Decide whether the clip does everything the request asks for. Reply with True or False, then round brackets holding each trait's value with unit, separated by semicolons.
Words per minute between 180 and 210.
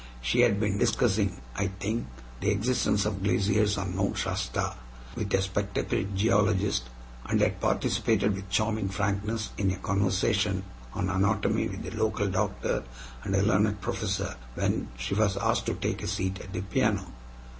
False (160 wpm)